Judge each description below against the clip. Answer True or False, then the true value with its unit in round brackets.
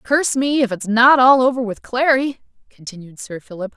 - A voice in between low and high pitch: False (240 Hz)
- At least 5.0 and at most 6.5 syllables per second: True (5.3 syllables/s)